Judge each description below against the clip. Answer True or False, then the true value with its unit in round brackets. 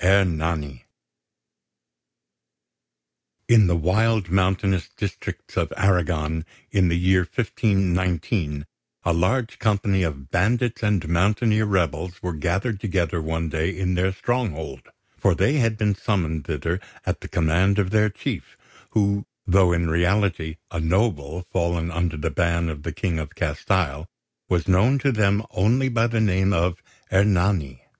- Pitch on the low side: True (90 Hz)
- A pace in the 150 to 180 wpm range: False (140 wpm)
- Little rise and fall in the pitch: False (3.5 semitones)